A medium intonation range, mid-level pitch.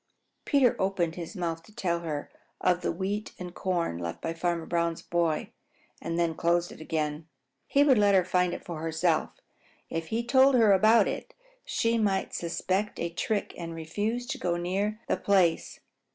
Yes: average, 3.7 semitones; medium, 175 Hz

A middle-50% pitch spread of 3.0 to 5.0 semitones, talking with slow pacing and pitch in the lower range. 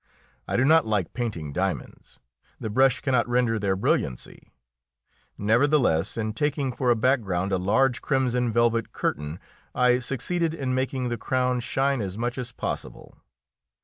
No: average, 3.7 semitones; average, 145 wpm; low, 120 Hz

